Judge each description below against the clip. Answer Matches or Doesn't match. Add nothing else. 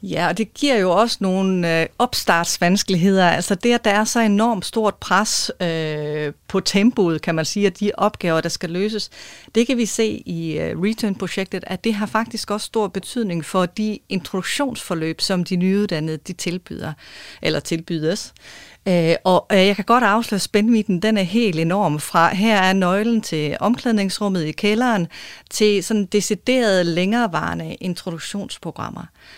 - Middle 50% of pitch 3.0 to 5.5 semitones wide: Matches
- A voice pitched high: Matches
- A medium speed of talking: Matches